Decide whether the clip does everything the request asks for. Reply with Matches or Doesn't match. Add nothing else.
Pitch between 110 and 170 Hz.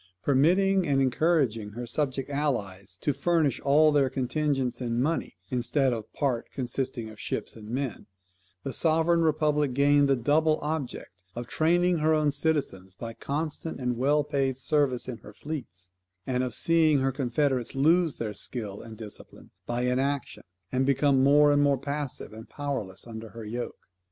Matches